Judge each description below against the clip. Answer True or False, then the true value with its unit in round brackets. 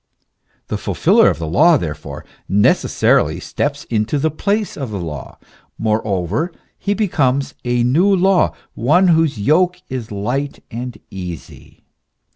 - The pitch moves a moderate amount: False (7.9 semitones)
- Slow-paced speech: True (130 wpm)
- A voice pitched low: True (130 Hz)